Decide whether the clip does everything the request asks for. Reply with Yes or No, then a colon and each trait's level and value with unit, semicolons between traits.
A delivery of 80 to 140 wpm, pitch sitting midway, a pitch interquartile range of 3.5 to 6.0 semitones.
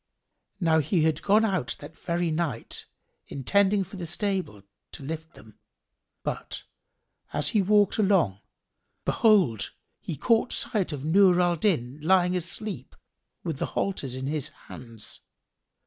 Yes: slow, 135 wpm; medium, 170 Hz; average, 5.2 semitones